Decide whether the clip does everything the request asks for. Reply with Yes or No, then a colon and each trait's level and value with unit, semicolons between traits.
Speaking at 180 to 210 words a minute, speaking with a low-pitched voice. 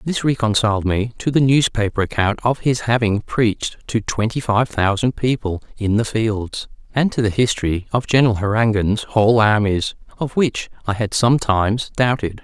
No: average, 165 wpm; low, 110 Hz